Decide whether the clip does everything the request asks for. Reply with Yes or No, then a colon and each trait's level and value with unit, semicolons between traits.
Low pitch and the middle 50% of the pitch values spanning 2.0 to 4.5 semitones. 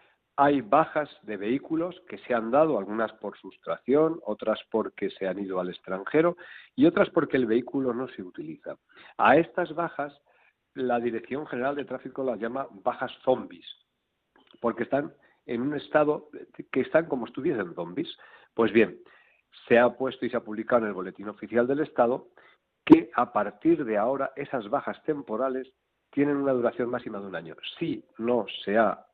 Yes: low, 130 Hz; average, 4.2 semitones